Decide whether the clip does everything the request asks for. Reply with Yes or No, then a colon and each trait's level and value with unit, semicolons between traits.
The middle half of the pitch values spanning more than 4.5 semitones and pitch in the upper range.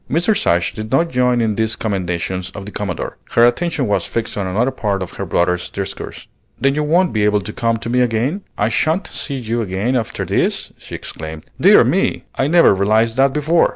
No: average, 5.1 semitones; low, 115 Hz